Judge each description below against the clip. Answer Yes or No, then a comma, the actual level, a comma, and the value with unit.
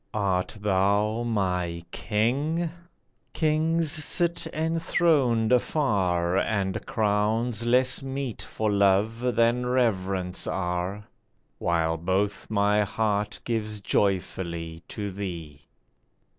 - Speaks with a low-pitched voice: Yes, low, 105 Hz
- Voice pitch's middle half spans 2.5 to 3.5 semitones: No, average, 4.6 semitones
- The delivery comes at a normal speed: No, slow, 90 wpm